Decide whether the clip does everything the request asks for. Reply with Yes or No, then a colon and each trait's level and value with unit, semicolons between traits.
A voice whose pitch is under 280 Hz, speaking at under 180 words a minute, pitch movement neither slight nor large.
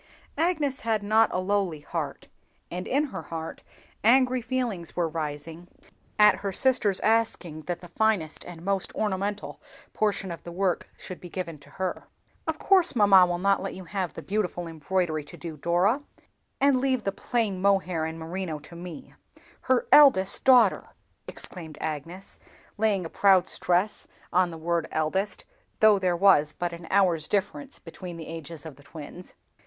Yes: medium, 185 Hz; average, 165 wpm; average, 4.1 semitones